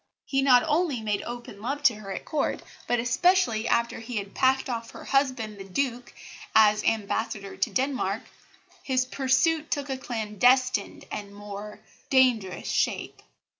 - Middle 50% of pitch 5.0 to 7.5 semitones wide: No, average, 4.0 semitones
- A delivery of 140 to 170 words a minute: Yes, average, 150 wpm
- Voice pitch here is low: No, high, 240 Hz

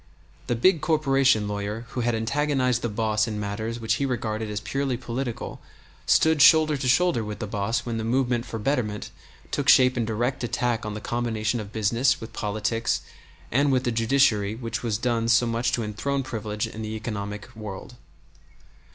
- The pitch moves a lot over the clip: No, average, 2.9 semitones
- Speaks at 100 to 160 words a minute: No, average, 180 wpm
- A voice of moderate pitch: No, low, 115 Hz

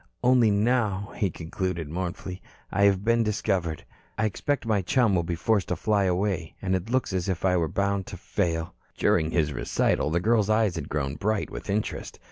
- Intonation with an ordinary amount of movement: Yes, average, 3.9 semitones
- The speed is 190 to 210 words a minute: Yes, average, 195 wpm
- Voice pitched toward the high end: No, very low, 95 Hz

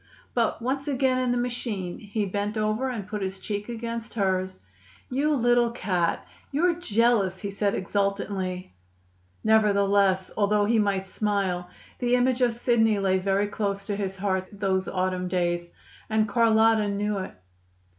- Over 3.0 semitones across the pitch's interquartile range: Yes, average, 3.4 semitones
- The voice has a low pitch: No, high, 205 Hz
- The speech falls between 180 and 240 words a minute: No, average, 150 wpm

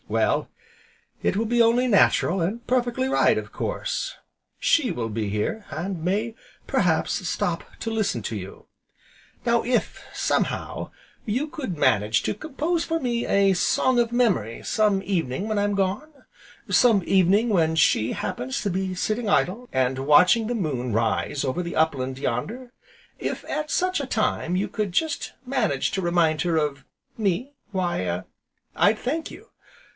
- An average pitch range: No, wide, 7.8 semitones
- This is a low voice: No, high, 195 Hz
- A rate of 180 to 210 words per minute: No, average, 155 wpm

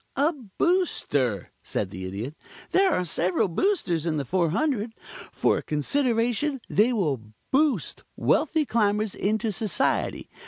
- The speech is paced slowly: Yes, slow, 125 wpm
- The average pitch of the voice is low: No, high, 210 Hz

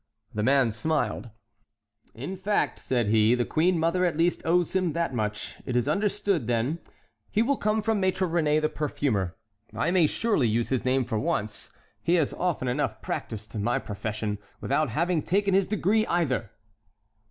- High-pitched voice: No, medium, 150 Hz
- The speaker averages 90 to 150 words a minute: No, average, 170 wpm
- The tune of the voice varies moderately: No, wide, 7.6 semitones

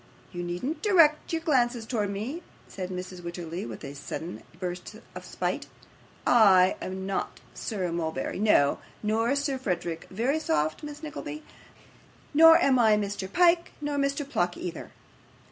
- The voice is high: Yes, high, 210 Hz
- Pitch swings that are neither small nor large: No, wide, 8.2 semitones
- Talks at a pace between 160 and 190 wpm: No, average, 145 wpm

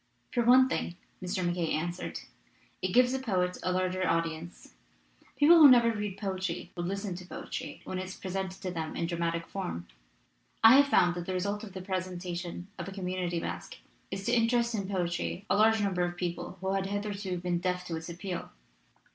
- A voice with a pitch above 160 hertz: Yes, medium, 185 Hz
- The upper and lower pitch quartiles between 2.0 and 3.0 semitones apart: Yes, narrow, 2.5 semitones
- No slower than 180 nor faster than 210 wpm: Yes, average, 195 wpm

